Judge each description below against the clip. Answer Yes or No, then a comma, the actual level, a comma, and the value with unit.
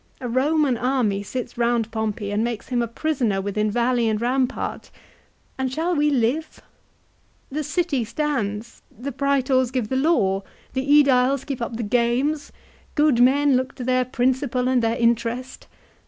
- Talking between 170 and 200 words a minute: No, average, 155 wpm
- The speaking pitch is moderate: No, very high, 250 Hz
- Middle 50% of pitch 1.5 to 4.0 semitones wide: Yes, average, 3.0 semitones